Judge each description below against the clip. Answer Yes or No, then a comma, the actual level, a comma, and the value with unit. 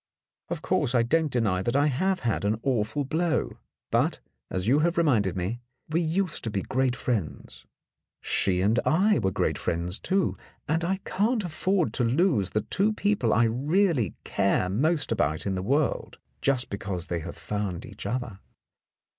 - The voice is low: Yes, low, 125 Hz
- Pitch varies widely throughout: Yes, wide, 8.4 semitones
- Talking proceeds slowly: No, average, 170 wpm